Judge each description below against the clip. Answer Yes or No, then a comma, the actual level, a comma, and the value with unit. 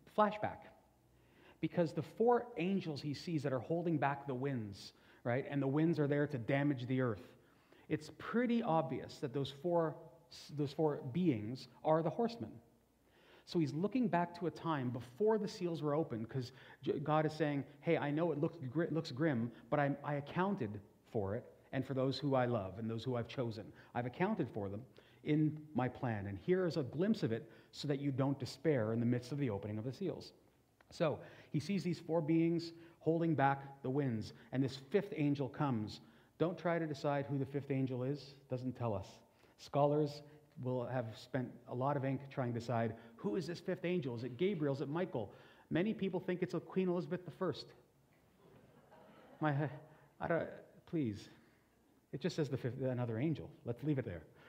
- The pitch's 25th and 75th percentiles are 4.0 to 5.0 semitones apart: Yes, average, 4.5 semitones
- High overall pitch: No, medium, 145 Hz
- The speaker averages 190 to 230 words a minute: Yes, average, 195 wpm